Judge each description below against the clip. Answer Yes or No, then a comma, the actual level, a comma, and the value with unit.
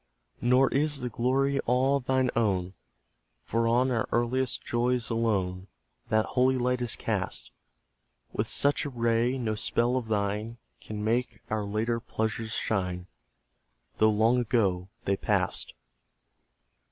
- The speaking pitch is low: Yes, low, 115 Hz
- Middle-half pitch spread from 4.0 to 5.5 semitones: No, narrow, 2.6 semitones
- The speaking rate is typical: No, slow, 130 wpm